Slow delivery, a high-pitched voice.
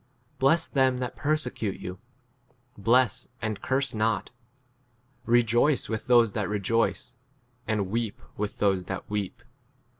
No: slow, 130 wpm; low, 115 Hz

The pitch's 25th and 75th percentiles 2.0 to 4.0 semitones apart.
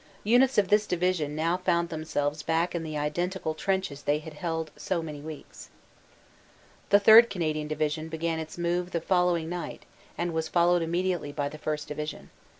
Yes: narrow, 2.6 semitones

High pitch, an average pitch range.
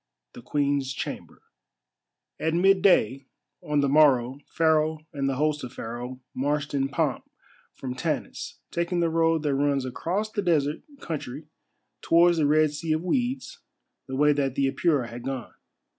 No: medium, 145 Hz; average, 3.3 semitones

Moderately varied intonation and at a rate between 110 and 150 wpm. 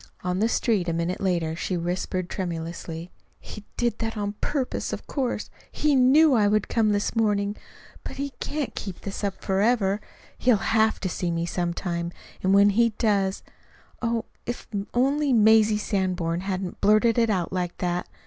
No: average, 4.1 semitones; average, 170 wpm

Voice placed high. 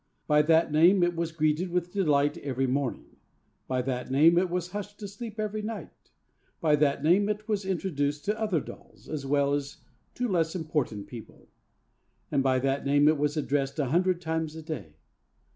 No: medium, 160 Hz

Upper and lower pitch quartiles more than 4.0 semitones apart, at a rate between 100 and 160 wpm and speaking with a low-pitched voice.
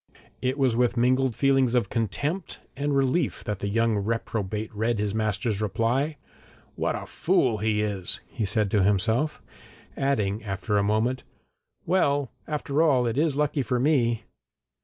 Yes: average, 4.4 semitones; average, 155 wpm; low, 115 Hz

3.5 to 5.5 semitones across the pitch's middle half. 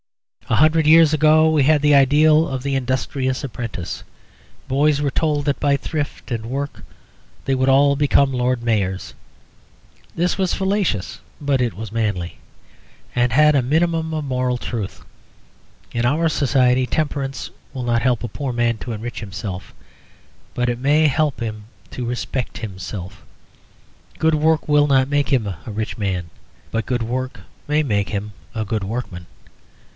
Yes: average, 4.4 semitones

